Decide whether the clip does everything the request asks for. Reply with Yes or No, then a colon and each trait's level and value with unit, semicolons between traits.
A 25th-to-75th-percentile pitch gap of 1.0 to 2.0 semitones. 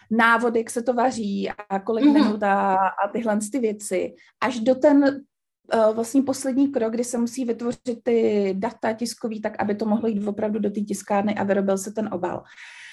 No: average, 2.8 semitones